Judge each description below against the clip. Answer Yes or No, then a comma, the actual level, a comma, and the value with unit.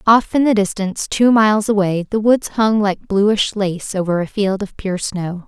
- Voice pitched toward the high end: Yes, high, 205 Hz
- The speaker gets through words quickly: Yes, fast, 210 wpm